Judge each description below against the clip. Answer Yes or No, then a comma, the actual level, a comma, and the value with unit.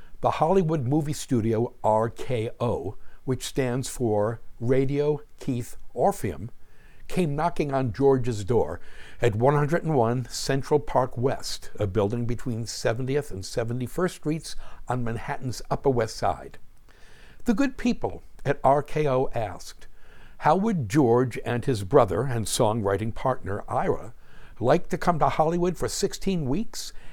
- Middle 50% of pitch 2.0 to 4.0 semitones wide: No, average, 4.4 semitones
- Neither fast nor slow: No, slow, 125 wpm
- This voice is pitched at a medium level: No, low, 130 Hz